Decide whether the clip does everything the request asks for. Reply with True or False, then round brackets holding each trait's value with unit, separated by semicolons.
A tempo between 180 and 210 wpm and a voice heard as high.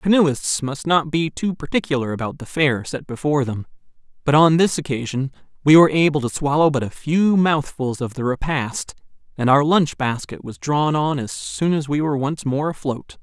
False (195 wpm; 145 Hz)